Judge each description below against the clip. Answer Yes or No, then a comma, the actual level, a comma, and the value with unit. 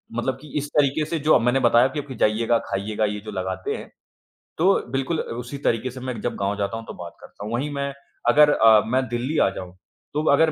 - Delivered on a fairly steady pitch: No, average, 4.7 semitones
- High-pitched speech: No, low, 120 Hz